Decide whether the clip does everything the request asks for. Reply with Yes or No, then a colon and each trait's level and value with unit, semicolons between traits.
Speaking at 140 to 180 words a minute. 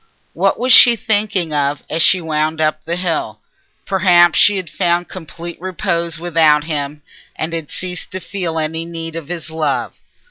Yes: average, 170 wpm